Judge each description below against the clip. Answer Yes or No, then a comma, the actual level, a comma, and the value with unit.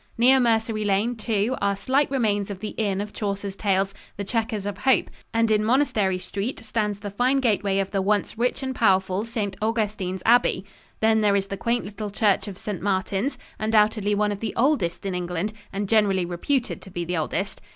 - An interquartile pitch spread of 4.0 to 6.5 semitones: No, narrow, 2.5 semitones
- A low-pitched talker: No, high, 210 Hz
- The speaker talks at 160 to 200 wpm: Yes, average, 195 wpm